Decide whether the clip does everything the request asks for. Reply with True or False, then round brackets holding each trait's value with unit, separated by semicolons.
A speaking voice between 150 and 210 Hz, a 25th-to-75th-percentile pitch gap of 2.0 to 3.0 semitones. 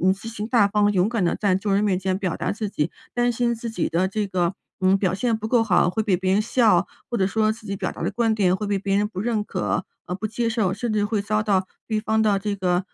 True (205 Hz; 2.6 semitones)